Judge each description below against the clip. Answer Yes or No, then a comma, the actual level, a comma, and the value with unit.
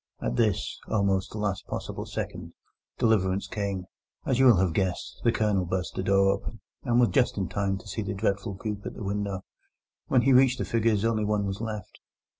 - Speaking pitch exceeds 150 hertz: No, low, 100 Hz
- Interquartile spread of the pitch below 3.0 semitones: Yes, narrow, 2.6 semitones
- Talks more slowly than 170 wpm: No, fast, 205 wpm